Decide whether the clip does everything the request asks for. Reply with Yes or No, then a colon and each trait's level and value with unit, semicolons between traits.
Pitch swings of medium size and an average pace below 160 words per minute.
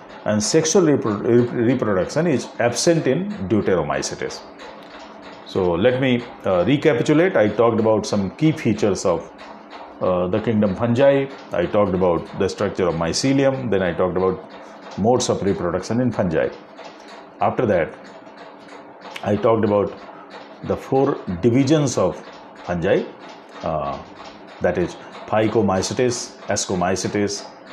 Yes: average, 4.7 semitones; average, 115 wpm